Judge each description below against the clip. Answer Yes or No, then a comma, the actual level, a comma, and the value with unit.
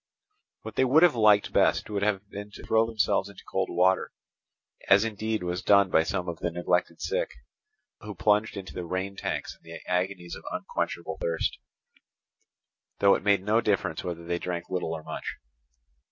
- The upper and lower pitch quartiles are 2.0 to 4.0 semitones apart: Yes, average, 3.1 semitones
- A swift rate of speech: No, average, 180 wpm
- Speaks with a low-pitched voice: Yes, low, 100 Hz